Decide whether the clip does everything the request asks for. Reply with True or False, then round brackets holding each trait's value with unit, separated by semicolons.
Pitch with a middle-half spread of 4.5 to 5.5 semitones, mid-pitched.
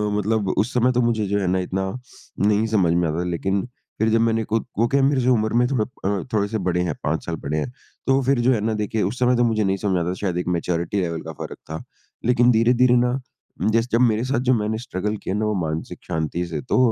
False (4.8 semitones; 105 Hz)